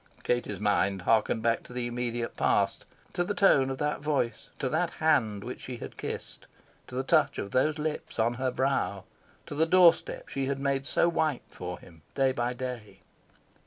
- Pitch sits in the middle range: No, low, 130 Hz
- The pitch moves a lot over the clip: No, average, 3.8 semitones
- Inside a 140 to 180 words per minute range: No, average, 195 wpm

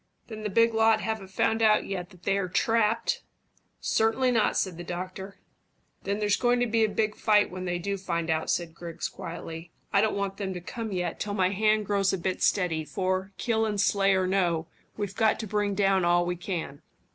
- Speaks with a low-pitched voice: No, high, 195 Hz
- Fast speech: Yes, fast, 215 wpm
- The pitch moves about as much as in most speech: Yes, average, 3.1 semitones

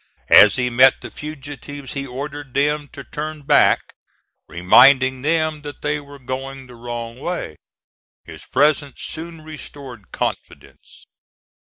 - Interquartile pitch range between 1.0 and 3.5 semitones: Yes, narrow, 2.6 semitones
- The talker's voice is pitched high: No, medium, 140 Hz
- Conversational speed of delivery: No, slow, 130 wpm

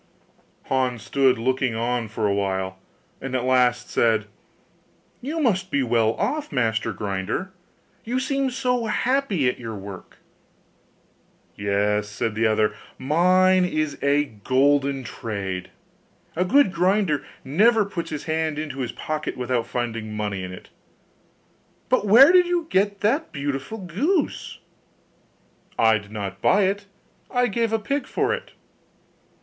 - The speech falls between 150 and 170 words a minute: No, average, 140 wpm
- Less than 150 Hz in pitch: Yes, medium, 140 Hz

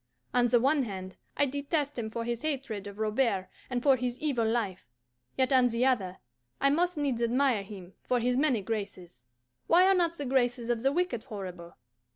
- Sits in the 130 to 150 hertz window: No, high, 245 Hz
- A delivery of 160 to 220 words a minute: Yes, average, 195 wpm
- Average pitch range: Yes, average, 4.3 semitones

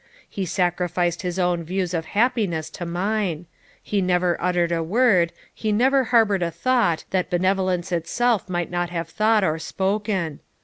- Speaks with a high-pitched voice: No, medium, 180 Hz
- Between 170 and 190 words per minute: No, average, 160 wpm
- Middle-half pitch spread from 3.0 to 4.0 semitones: Yes, average, 3.3 semitones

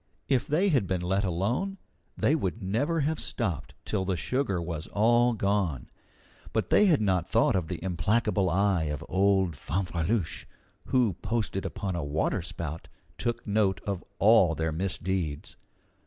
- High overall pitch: No, very low, 95 Hz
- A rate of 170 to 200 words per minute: No, average, 155 wpm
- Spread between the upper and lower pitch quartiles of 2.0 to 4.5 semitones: No, average, 4.9 semitones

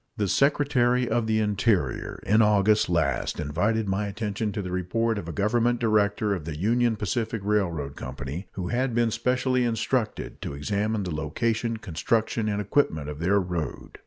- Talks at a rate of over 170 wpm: No, average, 165 wpm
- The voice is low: Yes, low, 105 Hz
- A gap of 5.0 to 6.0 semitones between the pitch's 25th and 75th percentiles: No, average, 4.3 semitones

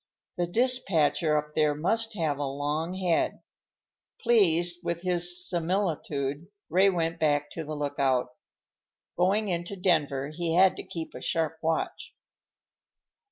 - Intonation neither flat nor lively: Yes, average, 3.2 semitones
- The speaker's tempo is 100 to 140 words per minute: Yes, slow, 135 wpm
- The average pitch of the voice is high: No, medium, 165 Hz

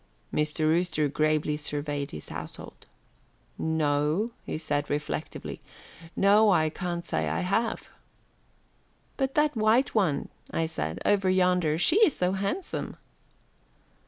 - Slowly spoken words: Yes, slow, 125 wpm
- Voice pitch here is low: No, medium, 170 Hz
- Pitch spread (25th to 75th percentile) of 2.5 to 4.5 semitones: No, average, 5.1 semitones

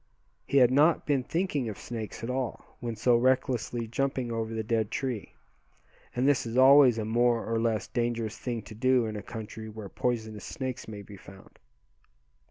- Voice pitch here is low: Yes, low, 120 Hz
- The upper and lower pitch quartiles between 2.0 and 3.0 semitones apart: Yes, narrow, 2.6 semitones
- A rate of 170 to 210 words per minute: Yes, average, 180 wpm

